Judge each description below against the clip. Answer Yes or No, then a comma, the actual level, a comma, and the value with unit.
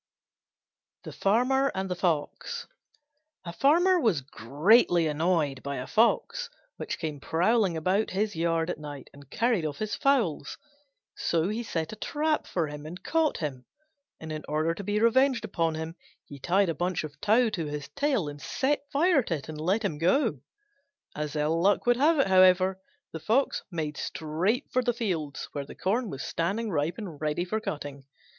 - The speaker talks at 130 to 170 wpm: No, average, 180 wpm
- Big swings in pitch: Yes, wide, 6.8 semitones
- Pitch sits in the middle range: Yes, medium, 175 Hz